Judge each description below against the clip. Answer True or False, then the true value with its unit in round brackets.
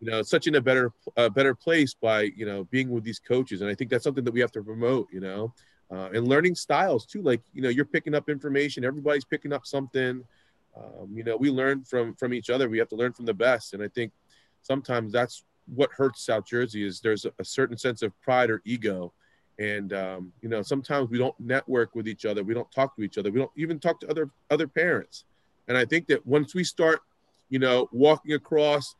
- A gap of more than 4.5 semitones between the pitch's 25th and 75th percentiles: False (4.0 semitones)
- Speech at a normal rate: False (240 wpm)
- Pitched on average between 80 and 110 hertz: False (125 Hz)